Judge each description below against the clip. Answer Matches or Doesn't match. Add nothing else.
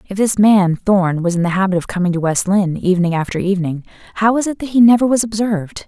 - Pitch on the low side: Doesn't match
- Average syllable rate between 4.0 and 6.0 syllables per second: Doesn't match